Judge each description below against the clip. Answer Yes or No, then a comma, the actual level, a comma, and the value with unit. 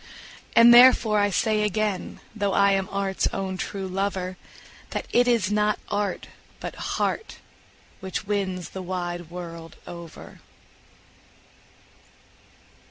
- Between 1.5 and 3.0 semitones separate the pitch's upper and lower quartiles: Yes, narrow, 2.4 semitones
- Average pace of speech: No, slow, 115 wpm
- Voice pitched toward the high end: Yes, high, 195 Hz